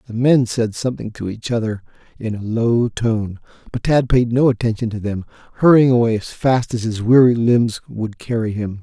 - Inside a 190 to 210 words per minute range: Yes, average, 195 wpm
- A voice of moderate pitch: No, low, 115 Hz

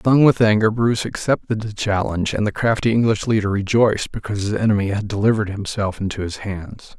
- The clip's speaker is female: No, male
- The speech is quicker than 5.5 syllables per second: Yes, 6.1 syllables/s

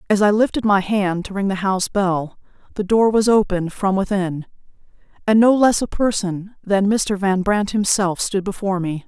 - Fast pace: No, average, 190 wpm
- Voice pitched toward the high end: Yes, high, 200 Hz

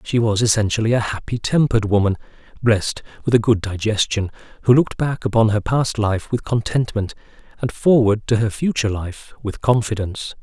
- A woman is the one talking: No, male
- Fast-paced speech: No, average, 165 wpm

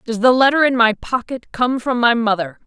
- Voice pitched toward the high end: Yes, high, 240 Hz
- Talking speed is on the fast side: Yes, fast, 225 wpm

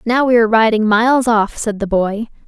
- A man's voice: No, female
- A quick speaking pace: Yes, fast, 220 wpm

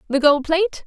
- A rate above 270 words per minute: No, fast, 210 wpm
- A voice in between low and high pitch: No, very high, 315 Hz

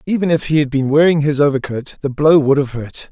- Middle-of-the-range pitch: Yes, medium, 145 Hz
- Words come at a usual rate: No, fast, 250 wpm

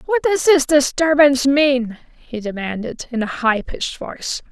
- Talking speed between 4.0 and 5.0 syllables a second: Yes, 4.6 syllables/s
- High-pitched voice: Yes, very high, 270 Hz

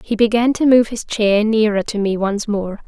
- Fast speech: Yes, fast, 230 wpm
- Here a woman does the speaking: Yes, female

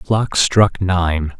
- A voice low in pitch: Yes, very low, 95 Hz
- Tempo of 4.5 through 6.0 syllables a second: No, 3.1 syllables/s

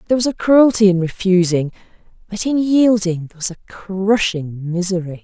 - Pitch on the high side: Yes, high, 195 Hz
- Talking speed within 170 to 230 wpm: No, average, 160 wpm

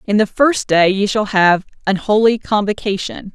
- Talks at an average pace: Yes, average, 180 wpm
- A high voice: Yes, high, 205 Hz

